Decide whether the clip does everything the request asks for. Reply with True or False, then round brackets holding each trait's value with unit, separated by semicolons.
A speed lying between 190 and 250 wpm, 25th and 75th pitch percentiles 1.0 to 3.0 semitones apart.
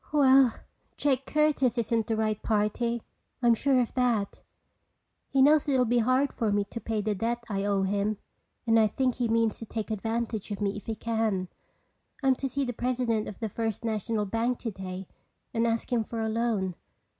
True (195 wpm; 2.7 semitones)